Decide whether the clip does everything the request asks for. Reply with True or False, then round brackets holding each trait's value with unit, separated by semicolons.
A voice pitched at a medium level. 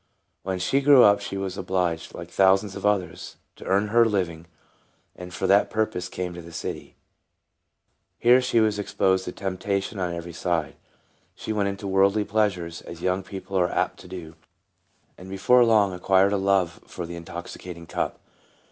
False (95 Hz)